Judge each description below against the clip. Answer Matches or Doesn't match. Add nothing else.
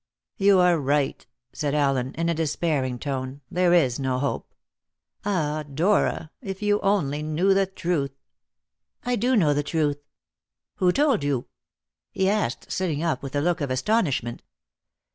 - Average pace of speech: Matches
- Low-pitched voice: Doesn't match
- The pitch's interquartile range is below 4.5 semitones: Doesn't match